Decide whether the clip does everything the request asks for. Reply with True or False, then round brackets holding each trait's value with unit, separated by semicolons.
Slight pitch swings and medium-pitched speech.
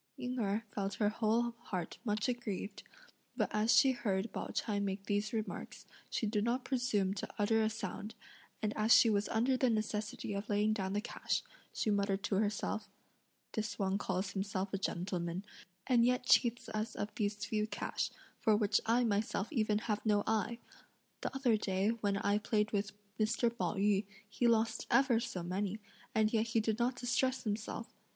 False (2.3 semitones; 215 Hz)